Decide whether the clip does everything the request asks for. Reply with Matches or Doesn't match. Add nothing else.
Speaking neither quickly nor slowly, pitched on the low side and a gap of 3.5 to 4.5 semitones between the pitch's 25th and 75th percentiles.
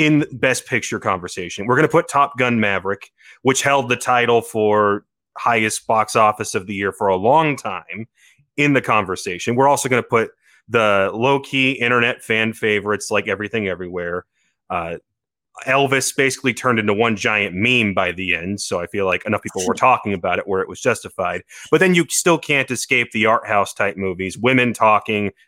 Matches